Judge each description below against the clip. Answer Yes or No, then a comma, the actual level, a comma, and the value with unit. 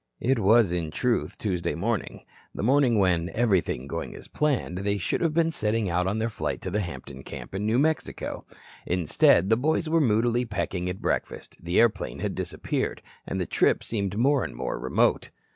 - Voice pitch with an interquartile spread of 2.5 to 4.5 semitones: No, average, 5.0 semitones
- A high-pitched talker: No, low, 105 Hz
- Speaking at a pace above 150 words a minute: Yes, average, 190 wpm